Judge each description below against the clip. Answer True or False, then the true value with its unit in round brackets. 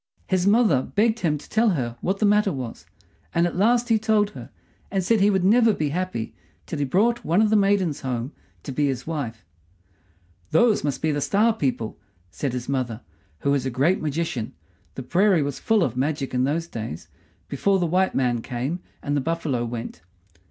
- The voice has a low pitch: False (160 Hz)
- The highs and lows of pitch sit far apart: True (7.4 semitones)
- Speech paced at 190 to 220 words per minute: True (200 wpm)